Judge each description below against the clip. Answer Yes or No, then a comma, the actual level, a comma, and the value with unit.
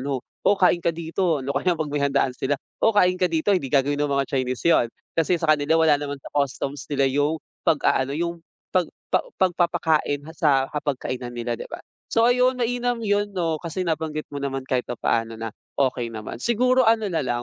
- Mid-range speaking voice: Yes, medium, 155 Hz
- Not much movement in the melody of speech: No, average, 4.8 semitones